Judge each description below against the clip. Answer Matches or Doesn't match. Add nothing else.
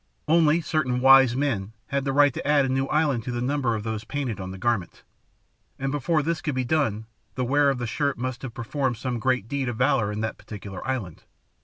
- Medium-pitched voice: Doesn't match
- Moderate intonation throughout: Matches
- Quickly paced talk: Matches